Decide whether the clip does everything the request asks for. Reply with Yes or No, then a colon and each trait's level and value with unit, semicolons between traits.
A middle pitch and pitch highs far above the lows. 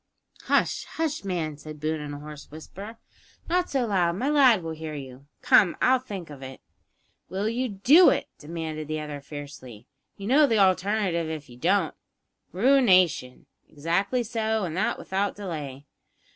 Yes: medium, 175 Hz; wide, 6.3 semitones